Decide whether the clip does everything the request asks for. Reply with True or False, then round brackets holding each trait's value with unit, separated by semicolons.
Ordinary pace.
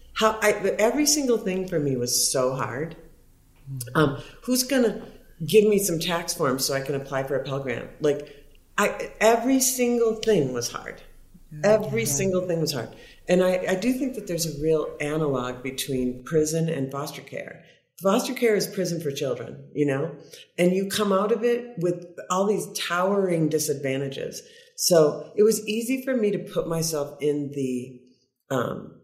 True (175 wpm)